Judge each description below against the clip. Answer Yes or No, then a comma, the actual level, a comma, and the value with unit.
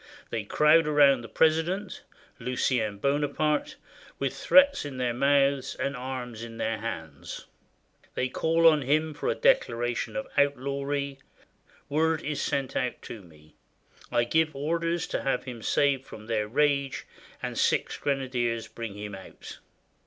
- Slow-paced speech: No, average, 145 wpm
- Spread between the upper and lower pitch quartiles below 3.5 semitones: No, average, 4.5 semitones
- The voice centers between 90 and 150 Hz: Yes, low, 135 Hz